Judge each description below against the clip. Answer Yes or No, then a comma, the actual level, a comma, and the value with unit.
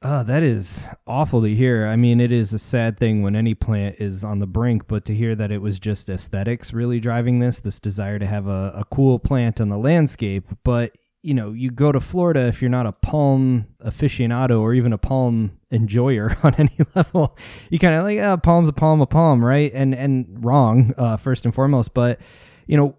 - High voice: No, low, 120 Hz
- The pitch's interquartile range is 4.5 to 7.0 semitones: No, average, 3.8 semitones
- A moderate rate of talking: No, fast, 220 wpm